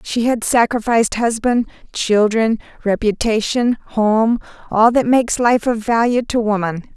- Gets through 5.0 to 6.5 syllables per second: No, 4.5 syllables/s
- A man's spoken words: No, female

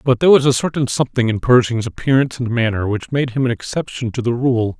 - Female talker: No, male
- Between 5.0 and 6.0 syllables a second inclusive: No, 6.4 syllables/s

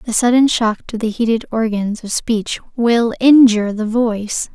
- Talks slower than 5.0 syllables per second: Yes, 4.6 syllables/s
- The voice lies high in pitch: Yes, high, 225 Hz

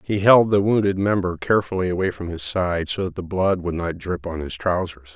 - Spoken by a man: Yes, male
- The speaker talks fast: Yes, fast, 235 wpm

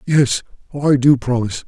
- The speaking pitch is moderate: No, low, 130 Hz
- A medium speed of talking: Yes, average, 145 wpm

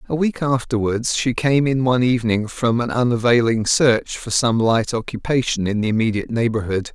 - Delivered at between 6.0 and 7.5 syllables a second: No, 5.3 syllables/s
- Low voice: Yes, low, 120 Hz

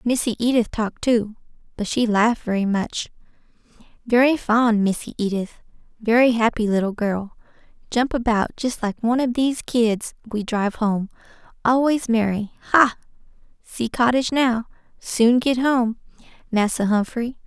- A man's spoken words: No, female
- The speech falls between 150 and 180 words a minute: No, slow, 135 wpm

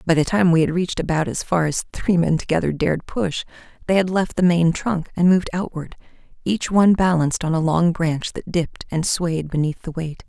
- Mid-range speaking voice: Yes, medium, 165 Hz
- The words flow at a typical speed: No, fast, 220 wpm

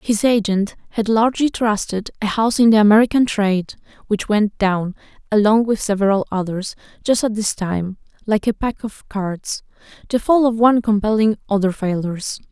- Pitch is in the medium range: No, high, 210 Hz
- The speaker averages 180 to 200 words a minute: No, average, 165 wpm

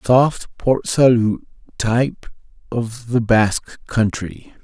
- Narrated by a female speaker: No, male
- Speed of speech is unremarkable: No, slow, 105 wpm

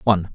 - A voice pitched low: Yes, very low, 95 Hz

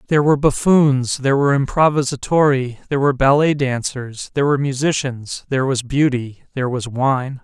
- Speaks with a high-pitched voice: No, low, 135 Hz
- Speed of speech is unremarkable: Yes, average, 155 wpm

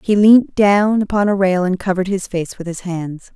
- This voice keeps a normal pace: No, fast, 235 wpm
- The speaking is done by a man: No, female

